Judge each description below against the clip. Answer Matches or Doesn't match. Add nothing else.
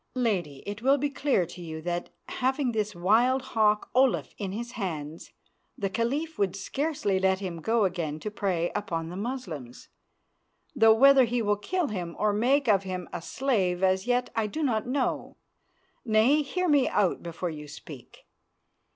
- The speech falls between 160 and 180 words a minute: Matches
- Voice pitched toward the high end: Matches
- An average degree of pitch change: Doesn't match